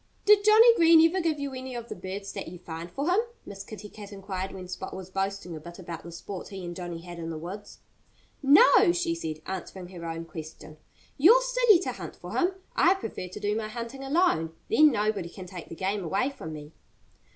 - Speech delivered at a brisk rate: Yes, fast, 220 wpm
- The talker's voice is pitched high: Yes, high, 195 Hz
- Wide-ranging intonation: Yes, wide, 8.7 semitones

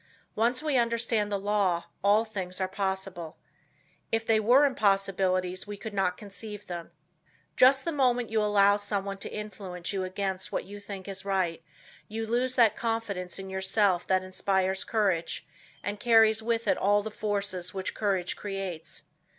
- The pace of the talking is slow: No, average, 160 wpm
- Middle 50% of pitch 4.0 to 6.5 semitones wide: No, narrow, 2.6 semitones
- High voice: Yes, high, 200 Hz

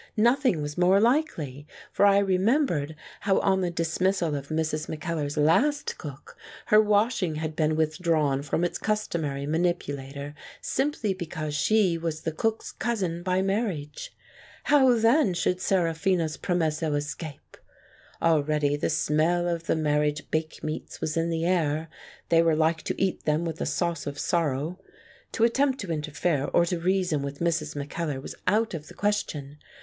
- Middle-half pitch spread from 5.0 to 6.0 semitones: No, average, 4.0 semitones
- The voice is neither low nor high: Yes, medium, 165 Hz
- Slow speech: No, average, 160 wpm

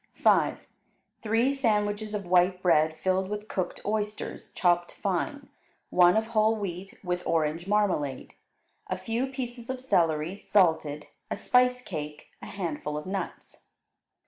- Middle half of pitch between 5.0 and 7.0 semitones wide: No, average, 4.1 semitones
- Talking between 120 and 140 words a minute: Yes, slow, 135 wpm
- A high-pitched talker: Yes, high, 195 Hz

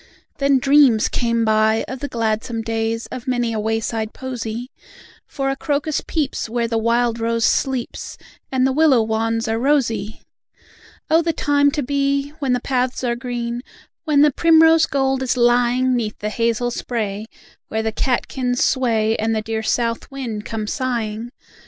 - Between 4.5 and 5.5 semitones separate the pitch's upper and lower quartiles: No, average, 3.1 semitones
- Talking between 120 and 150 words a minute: No, average, 165 wpm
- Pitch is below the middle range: No, high, 240 Hz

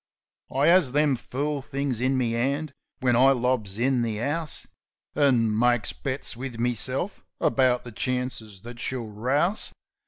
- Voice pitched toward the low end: Yes, low, 130 Hz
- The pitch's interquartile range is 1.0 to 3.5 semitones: Yes, average, 2.8 semitones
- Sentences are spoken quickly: No, average, 150 wpm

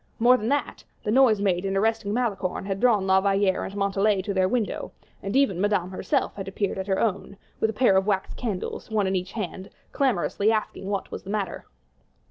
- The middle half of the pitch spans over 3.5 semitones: No, narrow, 2.4 semitones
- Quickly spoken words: Yes, fast, 210 wpm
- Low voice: No, high, 200 Hz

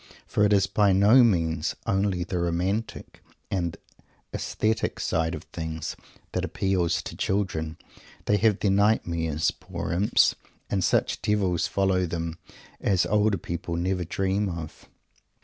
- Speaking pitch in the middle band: No, very low, 95 Hz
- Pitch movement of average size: Yes, average, 3.2 semitones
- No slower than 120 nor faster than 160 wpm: Yes, slow, 135 wpm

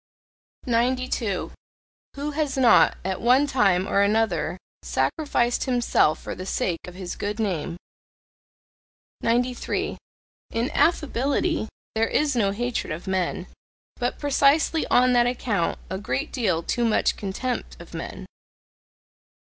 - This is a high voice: Yes, high, 235 Hz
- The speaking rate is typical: No, slow, 125 wpm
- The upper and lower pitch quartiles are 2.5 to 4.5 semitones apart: No, average, 5.1 semitones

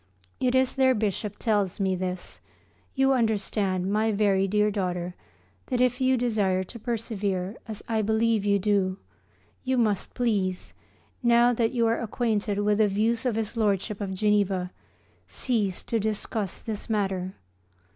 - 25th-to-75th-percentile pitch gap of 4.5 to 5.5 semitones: No, average, 3.0 semitones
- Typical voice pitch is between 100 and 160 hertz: No, high, 210 Hz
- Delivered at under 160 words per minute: Yes, average, 150 wpm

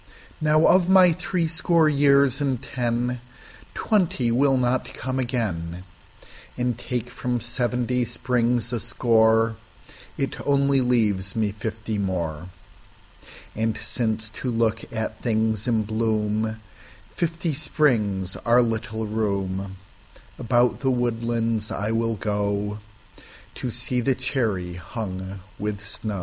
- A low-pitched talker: Yes, low, 115 Hz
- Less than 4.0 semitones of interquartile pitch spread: Yes, average, 3.0 semitones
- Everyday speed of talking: No, slow, 100 wpm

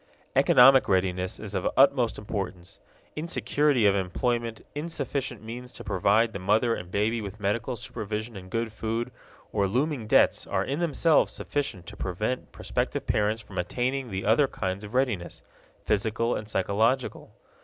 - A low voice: Yes, low, 110 Hz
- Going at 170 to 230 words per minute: No, average, 150 wpm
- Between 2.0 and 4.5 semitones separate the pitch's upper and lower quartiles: Yes, average, 4.0 semitones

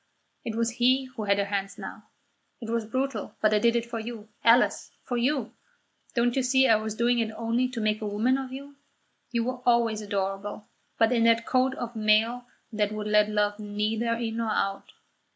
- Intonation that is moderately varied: No, narrow, 2.3 semitones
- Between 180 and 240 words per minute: Yes, fast, 205 wpm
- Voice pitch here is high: Yes, high, 230 Hz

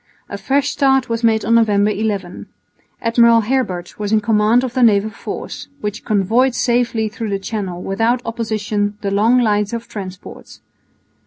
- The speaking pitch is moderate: No, high, 220 Hz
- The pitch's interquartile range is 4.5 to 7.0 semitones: No, narrow, 2.4 semitones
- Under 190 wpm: Yes, average, 160 wpm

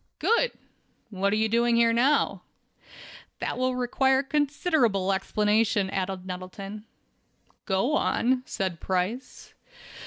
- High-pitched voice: Yes, high, 220 Hz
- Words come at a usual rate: No, slow, 105 wpm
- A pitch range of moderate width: Yes, average, 4.9 semitones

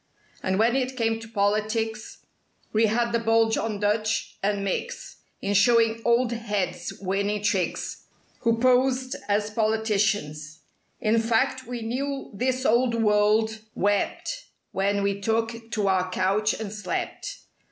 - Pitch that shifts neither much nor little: No, narrow, 2.3 semitones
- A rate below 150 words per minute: Yes, average, 140 wpm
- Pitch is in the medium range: No, high, 220 Hz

